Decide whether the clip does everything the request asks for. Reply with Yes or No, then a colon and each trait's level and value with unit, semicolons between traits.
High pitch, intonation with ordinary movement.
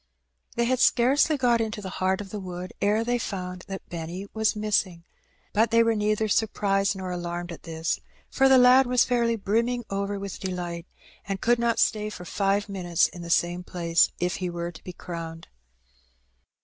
Yes: high, 195 Hz; average, 4.3 semitones